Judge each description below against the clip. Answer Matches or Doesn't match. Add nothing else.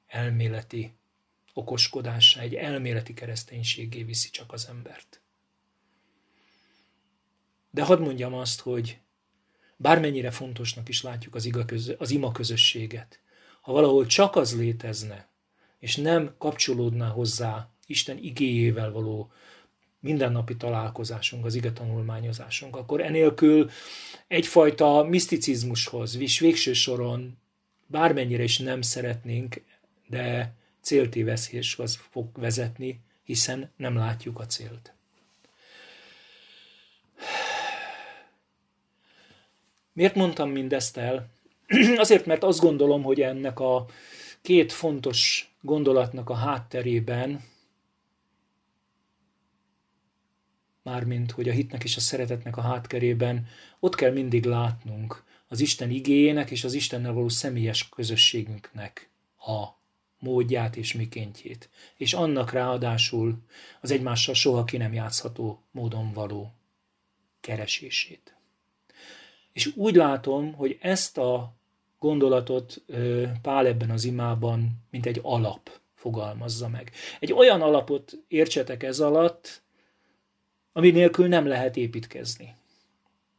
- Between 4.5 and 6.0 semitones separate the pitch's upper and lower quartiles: Doesn't match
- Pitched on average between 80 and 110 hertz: Doesn't match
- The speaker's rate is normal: Doesn't match